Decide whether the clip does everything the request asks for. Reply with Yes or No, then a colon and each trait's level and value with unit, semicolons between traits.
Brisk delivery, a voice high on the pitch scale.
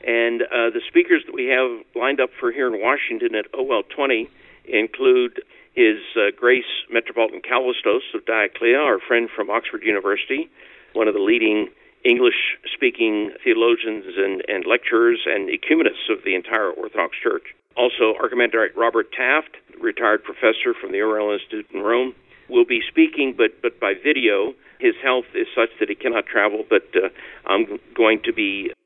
No: average, 165 wpm; very high, 370 Hz